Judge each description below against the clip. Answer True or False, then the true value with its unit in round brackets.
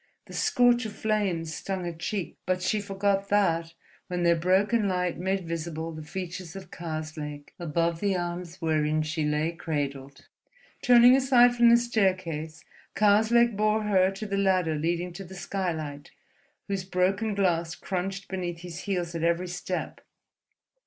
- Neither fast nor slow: True (150 wpm)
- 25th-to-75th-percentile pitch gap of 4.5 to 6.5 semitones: False (3.3 semitones)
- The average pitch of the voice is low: False (180 Hz)